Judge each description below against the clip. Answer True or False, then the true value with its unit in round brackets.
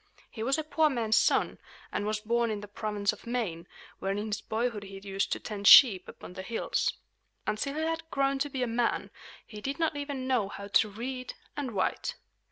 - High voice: True (225 Hz)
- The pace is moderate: False (210 wpm)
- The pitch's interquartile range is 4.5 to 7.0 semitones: True (4.8 semitones)